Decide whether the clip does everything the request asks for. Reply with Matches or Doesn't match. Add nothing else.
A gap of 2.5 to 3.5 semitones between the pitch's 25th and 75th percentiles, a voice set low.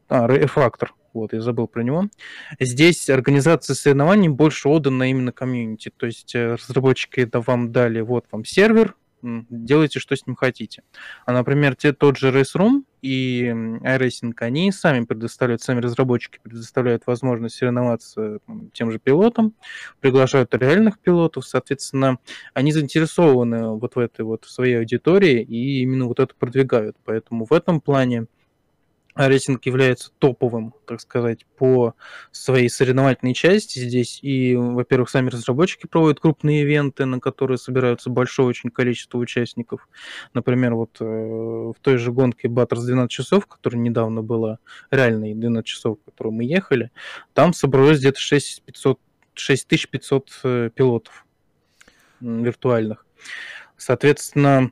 Matches